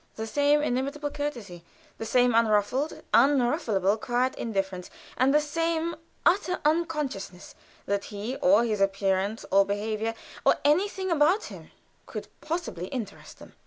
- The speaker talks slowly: Yes, slow, 130 wpm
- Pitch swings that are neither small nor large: No, wide, 6.5 semitones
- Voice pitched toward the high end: Yes, high, 245 Hz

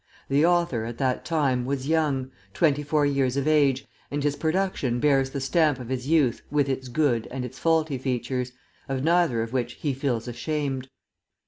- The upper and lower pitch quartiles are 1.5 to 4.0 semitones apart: Yes, average, 2.9 semitones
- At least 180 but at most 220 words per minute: Yes, average, 185 wpm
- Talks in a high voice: No, low, 135 Hz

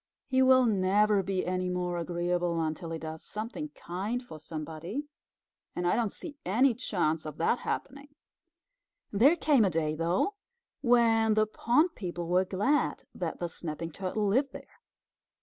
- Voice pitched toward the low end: No, high, 190 Hz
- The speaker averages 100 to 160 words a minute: Yes, average, 155 wpm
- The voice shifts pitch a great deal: Yes, wide, 5.8 semitones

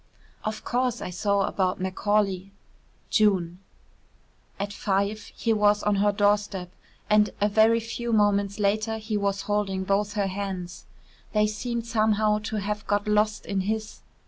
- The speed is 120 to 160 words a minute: Yes, average, 145 wpm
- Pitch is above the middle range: Yes, high, 205 Hz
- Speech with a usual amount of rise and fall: No, narrow, 1.3 semitones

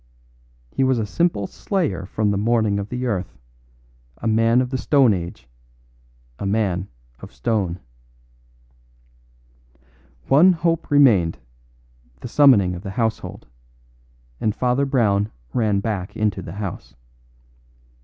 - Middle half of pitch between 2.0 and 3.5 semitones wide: No, average, 4.5 semitones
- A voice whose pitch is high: No, low, 110 Hz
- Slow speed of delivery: Yes, slow, 125 wpm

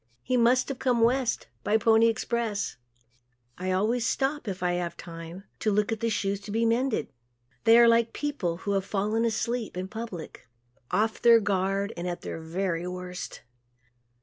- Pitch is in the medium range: No, high, 215 Hz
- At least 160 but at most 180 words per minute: Yes, average, 175 wpm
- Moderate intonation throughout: Yes, average, 3.9 semitones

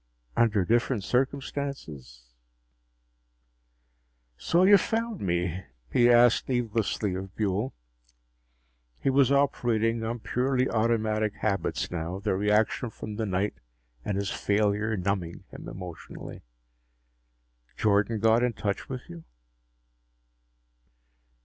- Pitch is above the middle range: No, low, 110 Hz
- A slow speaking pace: Yes, slow, 105 wpm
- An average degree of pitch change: Yes, average, 3.9 semitones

